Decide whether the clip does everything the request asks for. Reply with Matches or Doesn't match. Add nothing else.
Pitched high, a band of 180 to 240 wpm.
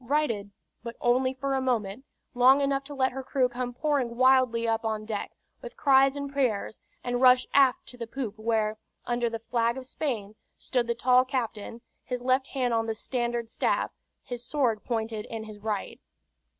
Matches